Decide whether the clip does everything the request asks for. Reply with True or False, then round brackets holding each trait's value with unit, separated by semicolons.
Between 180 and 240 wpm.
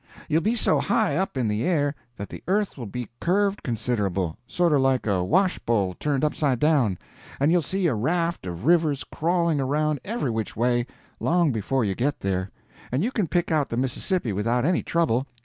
True (185 wpm)